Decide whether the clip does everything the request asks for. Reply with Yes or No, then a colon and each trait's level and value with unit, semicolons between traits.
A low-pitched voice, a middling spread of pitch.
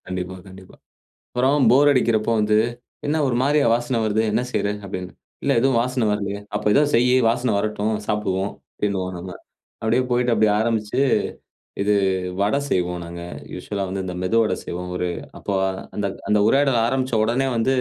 Yes: low, 110 Hz; average, 4.3 semitones